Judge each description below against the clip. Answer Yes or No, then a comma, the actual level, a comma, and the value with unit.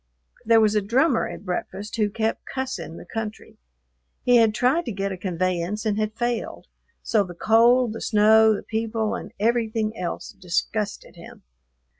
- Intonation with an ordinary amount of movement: No, narrow, 2.1 semitones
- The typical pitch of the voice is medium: No, high, 215 Hz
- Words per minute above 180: No, average, 165 wpm